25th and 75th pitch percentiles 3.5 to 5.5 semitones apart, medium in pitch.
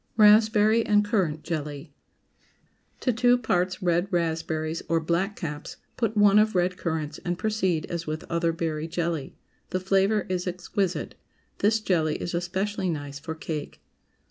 Yes: average, 4.3 semitones; medium, 175 Hz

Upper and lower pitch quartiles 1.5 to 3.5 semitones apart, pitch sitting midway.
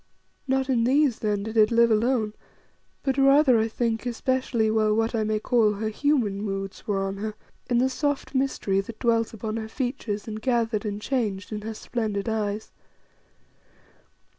No: average, 2.9 semitones; high, 225 Hz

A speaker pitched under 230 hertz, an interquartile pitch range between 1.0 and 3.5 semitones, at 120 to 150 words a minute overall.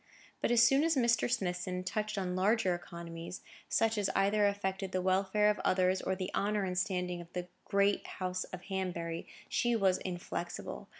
No: high, 190 Hz; narrow, 2.5 semitones; average, 175 wpm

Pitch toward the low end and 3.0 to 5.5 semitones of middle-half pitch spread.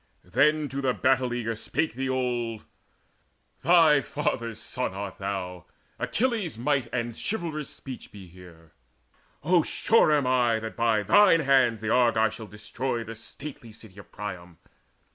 Yes: low, 120 Hz; average, 4.5 semitones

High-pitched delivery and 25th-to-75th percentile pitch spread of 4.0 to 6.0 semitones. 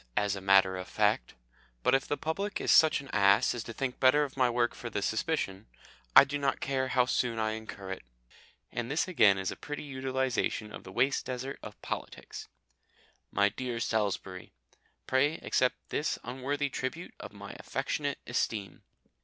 No: low, 125 Hz; average, 4.9 semitones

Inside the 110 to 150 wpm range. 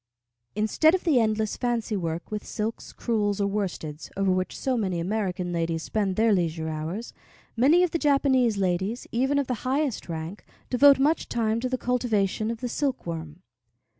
No: average, 170 wpm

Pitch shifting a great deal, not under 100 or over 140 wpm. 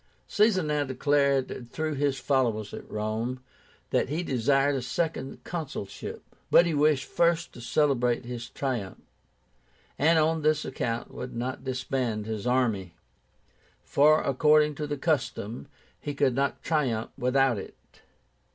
No: average, 3.9 semitones; slow, 135 wpm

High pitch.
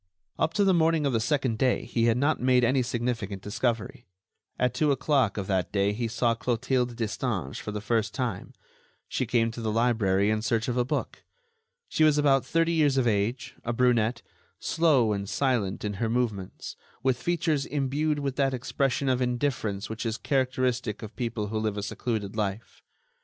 No: low, 120 Hz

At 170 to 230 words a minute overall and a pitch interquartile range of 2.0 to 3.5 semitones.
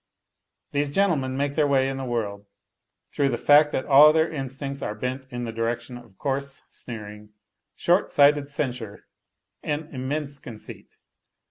No: average, 150 wpm; average, 3.1 semitones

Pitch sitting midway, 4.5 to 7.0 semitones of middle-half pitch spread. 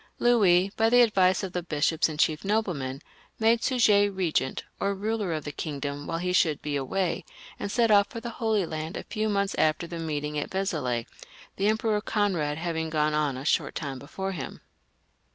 Yes: medium, 180 Hz; average, 5.3 semitones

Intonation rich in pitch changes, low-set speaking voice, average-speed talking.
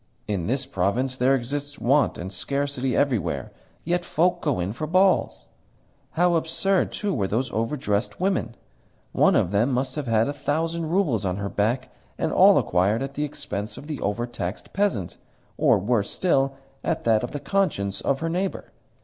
Yes: wide, 6.5 semitones; low, 130 Hz; average, 175 wpm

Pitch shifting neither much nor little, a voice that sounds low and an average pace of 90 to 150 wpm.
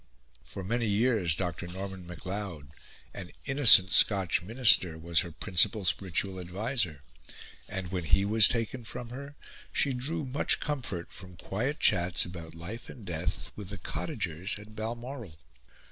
Yes: average, 4.9 semitones; very low, 95 Hz; average, 145 wpm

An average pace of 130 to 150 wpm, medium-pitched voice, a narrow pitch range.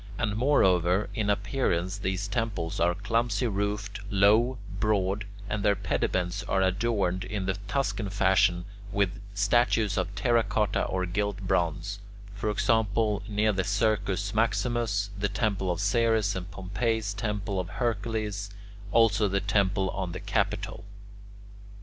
No: slow, 135 wpm; low, 100 Hz; narrow, 2.1 semitones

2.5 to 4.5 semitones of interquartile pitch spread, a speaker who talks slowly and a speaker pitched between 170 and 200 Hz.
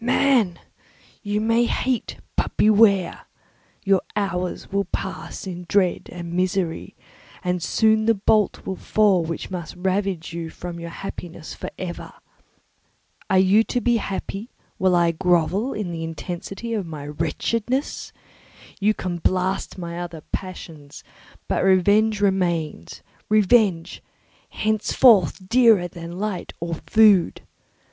Yes: average, 3.6 semitones; slow, 125 wpm; high, 190 Hz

